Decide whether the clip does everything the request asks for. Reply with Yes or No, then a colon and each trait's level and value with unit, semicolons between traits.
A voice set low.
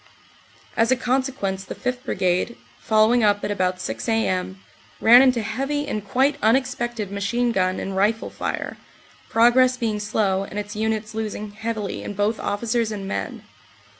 No: high, 220 Hz